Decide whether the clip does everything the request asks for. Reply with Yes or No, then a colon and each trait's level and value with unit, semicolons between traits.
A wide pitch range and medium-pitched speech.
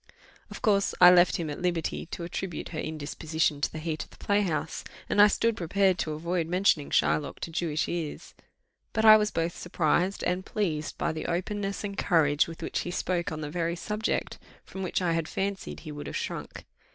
No: average, 3.4 semitones; medium, 175 Hz